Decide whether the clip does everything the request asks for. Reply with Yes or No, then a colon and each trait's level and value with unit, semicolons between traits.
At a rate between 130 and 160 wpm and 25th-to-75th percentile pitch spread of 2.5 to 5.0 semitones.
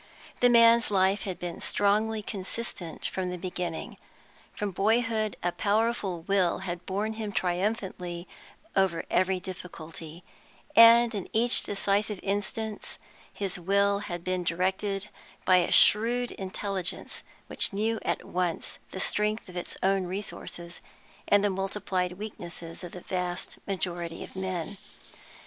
Yes: slow, 135 wpm; average, 2.8 semitones